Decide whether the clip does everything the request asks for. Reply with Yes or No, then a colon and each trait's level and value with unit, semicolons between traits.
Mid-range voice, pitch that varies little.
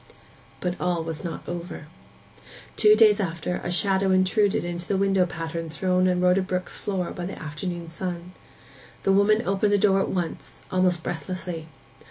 Yes: medium, 180 Hz; narrow, 2.0 semitones